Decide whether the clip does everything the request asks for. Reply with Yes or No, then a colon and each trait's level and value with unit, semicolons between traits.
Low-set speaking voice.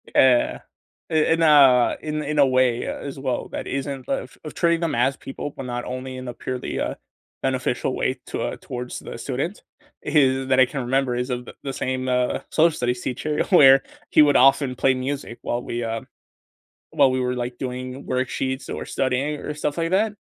Yes: low, 130 Hz